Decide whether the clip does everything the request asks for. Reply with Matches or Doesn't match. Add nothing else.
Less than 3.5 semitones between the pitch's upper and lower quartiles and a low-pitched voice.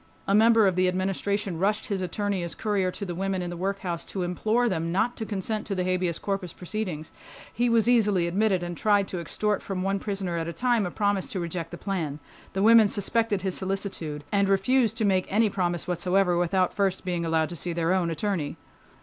Doesn't match